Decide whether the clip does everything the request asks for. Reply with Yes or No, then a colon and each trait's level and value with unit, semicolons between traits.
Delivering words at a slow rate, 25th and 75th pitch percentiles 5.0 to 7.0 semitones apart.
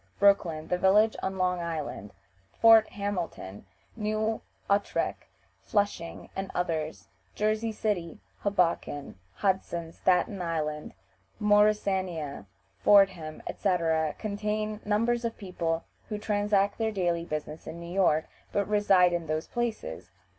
No: slow, 115 wpm; average, 4.0 semitones